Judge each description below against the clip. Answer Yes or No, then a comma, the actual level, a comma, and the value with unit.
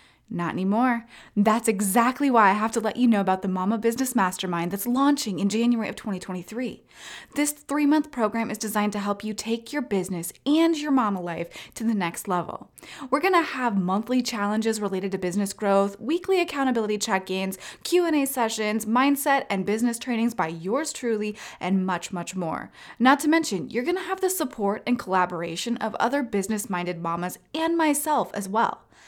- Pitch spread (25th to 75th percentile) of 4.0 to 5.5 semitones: Yes, average, 5.2 semitones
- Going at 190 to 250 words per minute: No, average, 175 wpm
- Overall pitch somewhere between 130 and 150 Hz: No, high, 220 Hz